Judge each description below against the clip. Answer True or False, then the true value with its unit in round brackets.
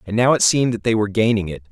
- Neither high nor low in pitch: False (110 Hz)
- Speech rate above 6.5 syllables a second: True (7.7 syllables/s)